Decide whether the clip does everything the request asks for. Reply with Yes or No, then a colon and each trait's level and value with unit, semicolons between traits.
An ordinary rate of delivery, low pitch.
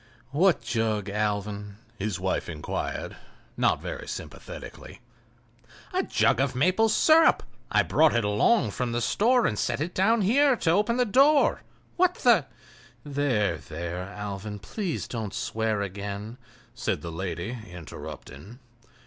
No: slow, 130 wpm; low, 110 Hz